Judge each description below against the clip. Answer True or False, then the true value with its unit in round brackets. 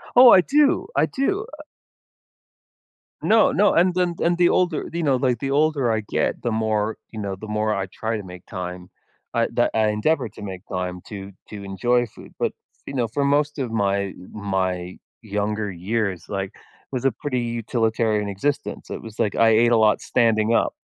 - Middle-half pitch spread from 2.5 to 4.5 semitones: False (5.4 semitones)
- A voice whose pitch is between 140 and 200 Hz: False (110 Hz)